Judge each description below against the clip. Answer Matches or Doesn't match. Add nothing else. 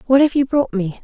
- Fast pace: Matches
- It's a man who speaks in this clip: Doesn't match